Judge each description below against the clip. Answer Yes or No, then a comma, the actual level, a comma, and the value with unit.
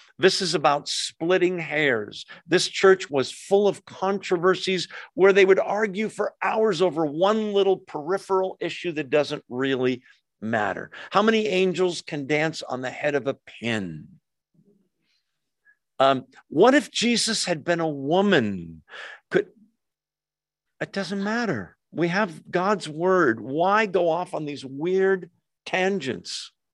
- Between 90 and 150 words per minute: Yes, slow, 135 wpm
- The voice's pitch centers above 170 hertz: Yes, medium, 185 Hz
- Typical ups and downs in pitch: Yes, average, 4.5 semitones